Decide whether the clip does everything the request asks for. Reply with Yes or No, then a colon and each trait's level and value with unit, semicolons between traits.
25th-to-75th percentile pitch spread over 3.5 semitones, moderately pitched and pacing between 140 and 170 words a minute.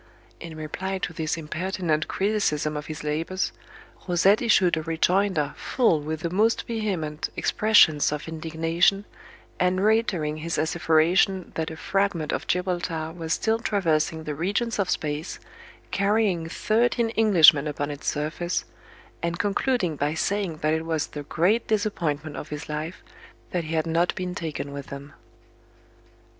Yes: average, 3.9 semitones; medium, 165 Hz; average, 145 wpm